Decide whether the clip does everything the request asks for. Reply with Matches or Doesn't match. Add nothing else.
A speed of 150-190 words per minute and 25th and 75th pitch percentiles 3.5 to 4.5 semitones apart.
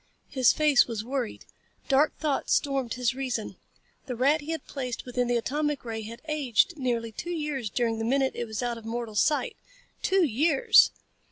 Matches